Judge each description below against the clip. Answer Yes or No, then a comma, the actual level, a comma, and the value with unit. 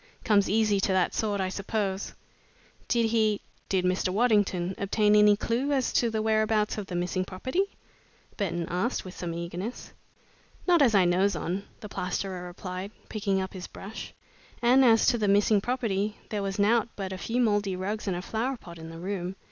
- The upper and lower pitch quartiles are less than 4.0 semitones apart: Yes, average, 2.9 semitones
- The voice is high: Yes, high, 200 Hz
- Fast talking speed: No, average, 190 wpm